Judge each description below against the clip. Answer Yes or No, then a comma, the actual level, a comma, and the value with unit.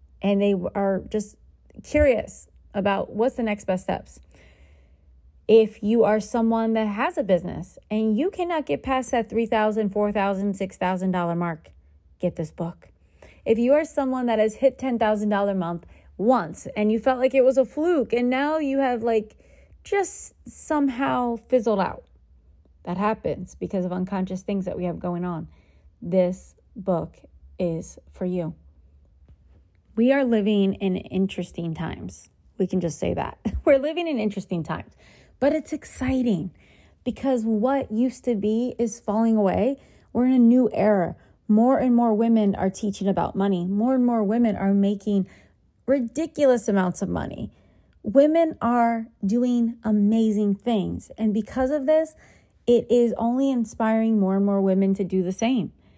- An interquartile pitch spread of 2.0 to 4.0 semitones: No, average, 4.8 semitones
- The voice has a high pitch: Yes, high, 215 Hz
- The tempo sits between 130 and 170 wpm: Yes, average, 160 wpm